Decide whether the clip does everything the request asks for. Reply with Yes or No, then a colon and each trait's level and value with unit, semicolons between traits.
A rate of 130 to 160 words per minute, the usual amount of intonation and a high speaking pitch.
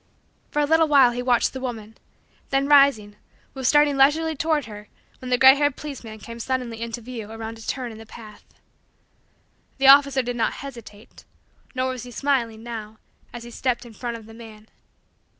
No: average, 185 wpm; average, 3.4 semitones; high, 245 Hz